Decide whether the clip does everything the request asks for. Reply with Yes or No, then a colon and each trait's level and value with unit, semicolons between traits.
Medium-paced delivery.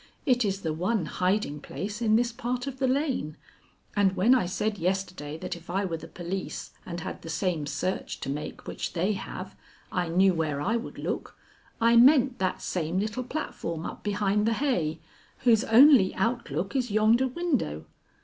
Yes: average, 180 wpm